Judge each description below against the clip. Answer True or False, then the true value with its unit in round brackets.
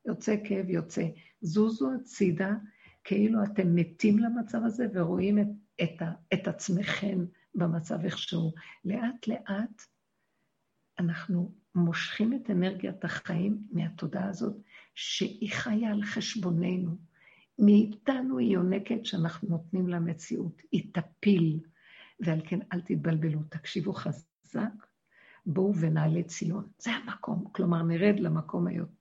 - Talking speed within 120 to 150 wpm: False (110 wpm)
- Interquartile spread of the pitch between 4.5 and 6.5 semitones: False (3.5 semitones)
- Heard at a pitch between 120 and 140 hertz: False (190 Hz)